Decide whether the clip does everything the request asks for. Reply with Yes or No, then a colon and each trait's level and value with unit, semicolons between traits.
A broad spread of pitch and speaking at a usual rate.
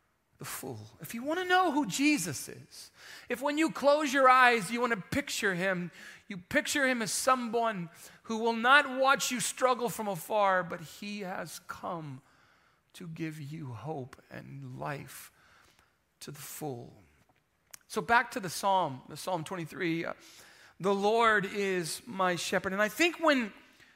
Yes: wide, 6.7 semitones; average, 165 wpm